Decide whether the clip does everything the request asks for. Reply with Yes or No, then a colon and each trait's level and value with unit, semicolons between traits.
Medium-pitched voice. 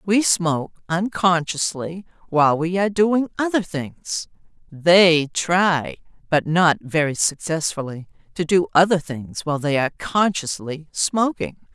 Yes: medium, 170 Hz